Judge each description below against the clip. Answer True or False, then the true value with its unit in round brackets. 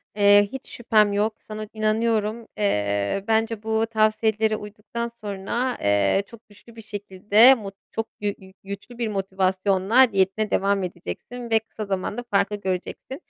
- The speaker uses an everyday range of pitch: False (2.3 semitones)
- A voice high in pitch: True (210 Hz)